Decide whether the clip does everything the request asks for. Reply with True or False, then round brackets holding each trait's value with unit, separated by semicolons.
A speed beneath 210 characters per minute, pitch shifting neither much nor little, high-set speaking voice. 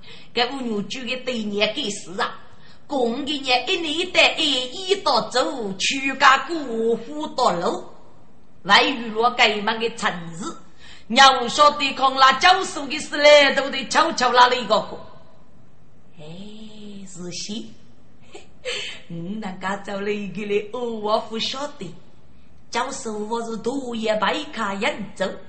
True (190 characters per minute; 4.6 semitones; 235 Hz)